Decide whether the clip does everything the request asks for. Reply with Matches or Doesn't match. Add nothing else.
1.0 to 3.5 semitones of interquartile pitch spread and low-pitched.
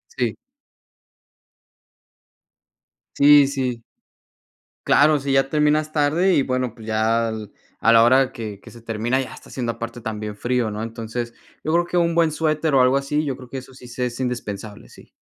Doesn't match